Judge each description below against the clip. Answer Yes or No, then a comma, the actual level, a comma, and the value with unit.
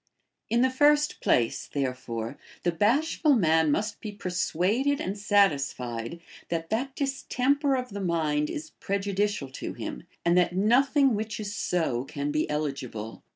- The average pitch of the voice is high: Yes, high, 195 Hz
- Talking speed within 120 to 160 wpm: Yes, average, 145 wpm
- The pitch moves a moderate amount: No, wide, 8.9 semitones